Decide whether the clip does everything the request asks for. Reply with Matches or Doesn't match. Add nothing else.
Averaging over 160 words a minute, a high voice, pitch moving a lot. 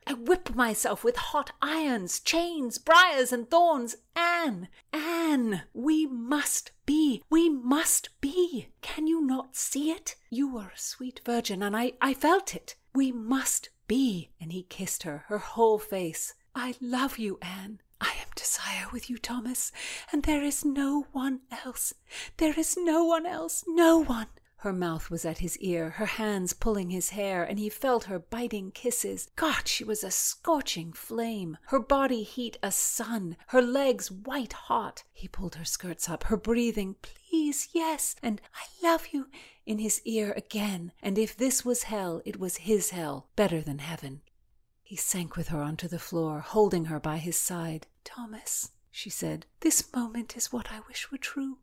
Matches